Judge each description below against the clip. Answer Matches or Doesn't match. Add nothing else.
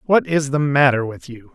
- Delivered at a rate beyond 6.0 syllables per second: Doesn't match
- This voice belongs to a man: Matches